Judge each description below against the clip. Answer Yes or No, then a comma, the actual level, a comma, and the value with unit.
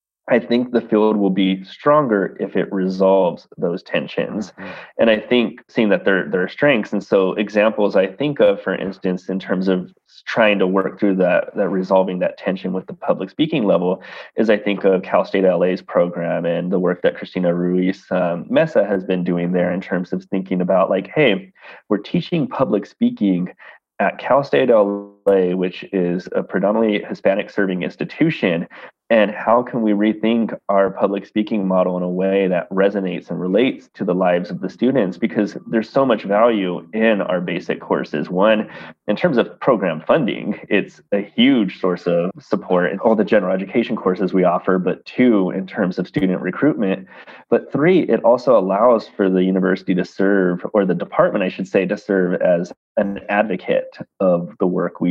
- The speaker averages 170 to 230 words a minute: Yes, average, 185 wpm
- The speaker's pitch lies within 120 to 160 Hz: No, very low, 95 Hz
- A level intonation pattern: Yes, narrow, 2.2 semitones